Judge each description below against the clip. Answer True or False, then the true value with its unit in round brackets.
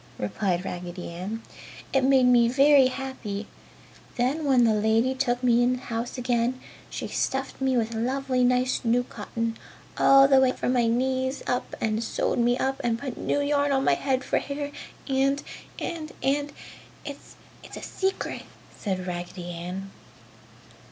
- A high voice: True (250 Hz)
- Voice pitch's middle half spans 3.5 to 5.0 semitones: False (3.0 semitones)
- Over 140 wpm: True (160 wpm)